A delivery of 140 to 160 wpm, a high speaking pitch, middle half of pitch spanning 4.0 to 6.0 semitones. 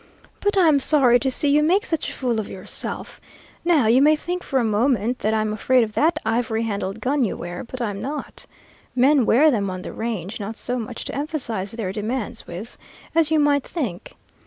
No: fast, 205 wpm; high, 245 Hz; average, 5.3 semitones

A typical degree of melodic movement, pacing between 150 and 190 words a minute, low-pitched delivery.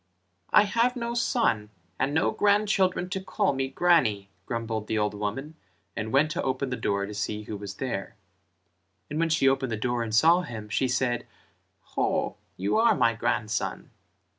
No: wide, 7.7 semitones; average, 175 wpm; low, 130 Hz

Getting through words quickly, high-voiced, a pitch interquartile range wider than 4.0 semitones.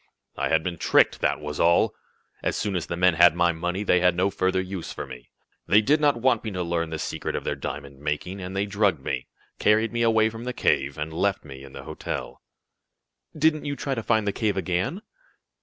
No: fast, 225 wpm; very low, 95 Hz; average, 5.0 semitones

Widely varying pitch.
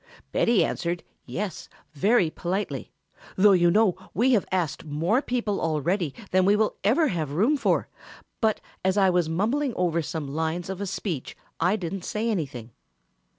No: average, 4.3 semitones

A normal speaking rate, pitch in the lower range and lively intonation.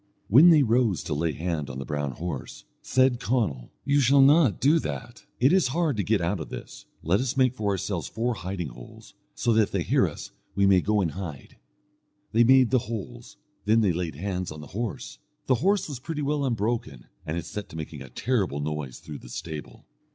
No: fast, 215 wpm; low, 105 Hz; wide, 8.0 semitones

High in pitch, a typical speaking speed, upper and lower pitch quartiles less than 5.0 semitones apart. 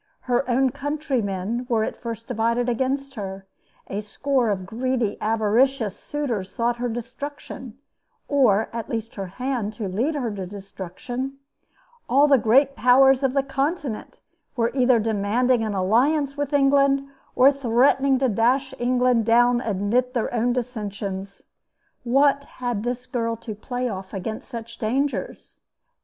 Yes: high, 245 Hz; average, 145 wpm; average, 3.6 semitones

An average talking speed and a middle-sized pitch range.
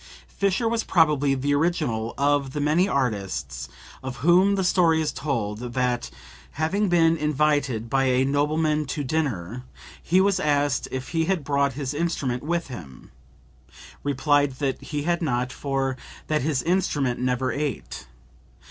Yes: average, 150 wpm; average, 4.0 semitones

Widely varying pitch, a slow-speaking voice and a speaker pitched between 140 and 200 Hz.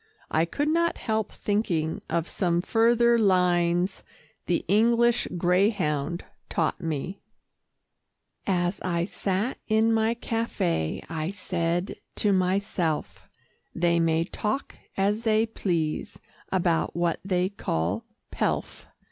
No: average, 4.4 semitones; slow, 110 wpm; medium, 185 Hz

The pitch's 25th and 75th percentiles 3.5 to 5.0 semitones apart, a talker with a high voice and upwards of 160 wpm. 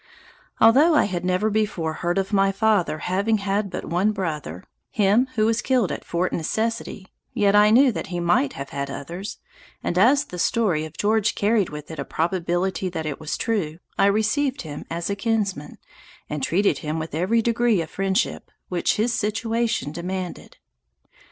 Yes: average, 4.5 semitones; high, 195 Hz; average, 175 wpm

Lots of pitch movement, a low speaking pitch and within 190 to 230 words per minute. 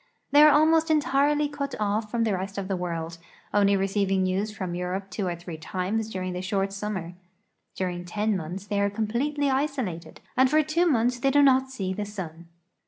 No: wide, 6.2 semitones; high, 205 Hz; average, 200 wpm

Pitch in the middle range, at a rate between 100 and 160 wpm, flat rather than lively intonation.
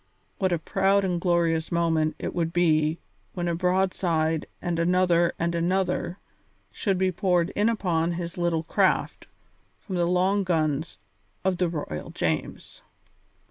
Yes: medium, 175 Hz; average, 140 wpm; narrow, 2.0 semitones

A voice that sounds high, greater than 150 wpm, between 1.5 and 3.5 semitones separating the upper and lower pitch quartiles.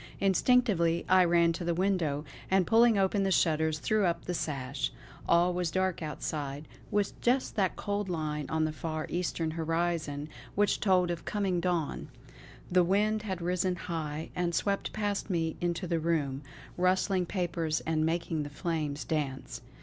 No: medium, 170 Hz; average, 160 wpm; average, 3.1 semitones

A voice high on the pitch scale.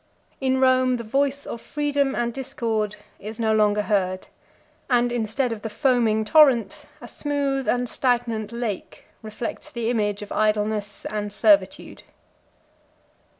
Yes: high, 235 Hz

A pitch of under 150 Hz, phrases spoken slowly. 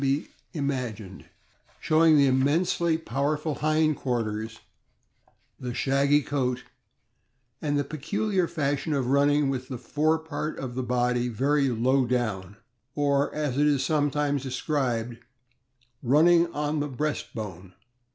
Yes: medium, 140 Hz; slow, 125 wpm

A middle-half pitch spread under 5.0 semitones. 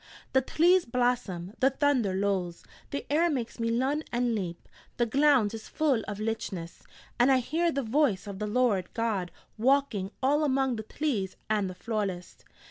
No: wide, 5.4 semitones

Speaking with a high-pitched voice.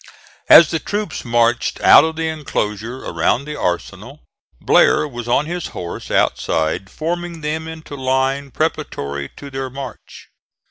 No: low, 135 Hz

